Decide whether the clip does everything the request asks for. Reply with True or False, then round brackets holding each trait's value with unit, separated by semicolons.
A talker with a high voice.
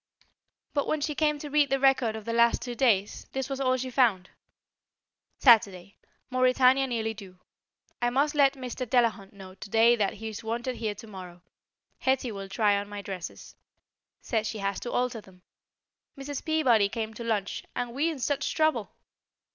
True (235 Hz)